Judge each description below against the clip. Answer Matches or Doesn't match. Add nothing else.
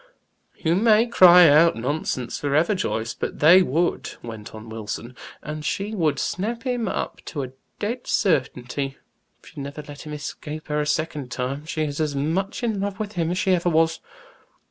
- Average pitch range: Matches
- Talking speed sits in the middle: Matches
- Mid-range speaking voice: Matches